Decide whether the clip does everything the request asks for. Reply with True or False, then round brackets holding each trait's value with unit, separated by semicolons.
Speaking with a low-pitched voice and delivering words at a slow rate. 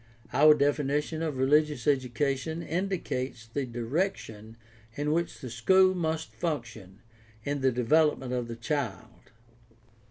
False (145 Hz; 120 wpm)